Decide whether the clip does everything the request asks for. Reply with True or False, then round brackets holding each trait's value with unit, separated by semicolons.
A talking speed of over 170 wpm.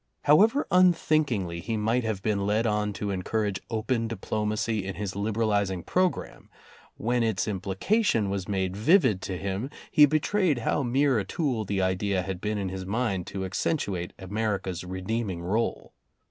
False (155 wpm)